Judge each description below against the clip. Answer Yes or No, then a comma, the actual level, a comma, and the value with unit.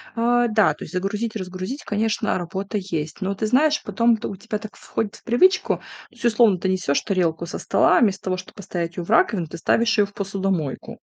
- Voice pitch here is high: Yes, high, 200 Hz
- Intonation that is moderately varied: Yes, average, 3.6 semitones